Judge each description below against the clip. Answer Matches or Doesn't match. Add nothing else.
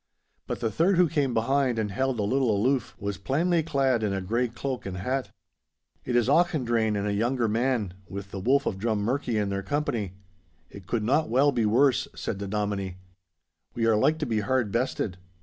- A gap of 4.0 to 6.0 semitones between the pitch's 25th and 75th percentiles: Matches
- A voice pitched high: Doesn't match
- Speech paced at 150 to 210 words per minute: Matches